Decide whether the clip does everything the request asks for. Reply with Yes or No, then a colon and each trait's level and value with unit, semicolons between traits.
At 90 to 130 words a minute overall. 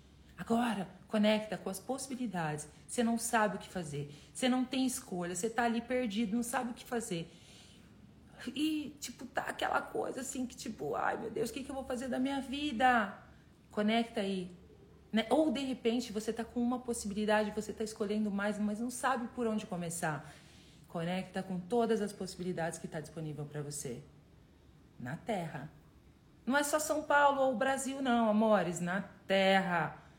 No: average, 175 wpm